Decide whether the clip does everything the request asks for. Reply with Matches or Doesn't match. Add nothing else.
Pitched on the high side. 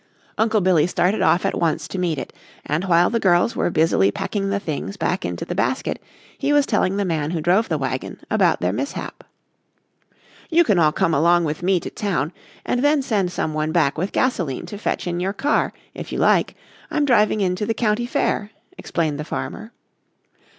Doesn't match